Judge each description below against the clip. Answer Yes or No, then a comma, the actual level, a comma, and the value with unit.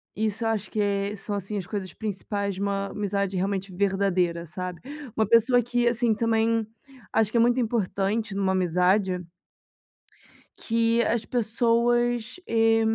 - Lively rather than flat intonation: No, average, 2.8 semitones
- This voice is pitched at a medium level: No, high, 210 Hz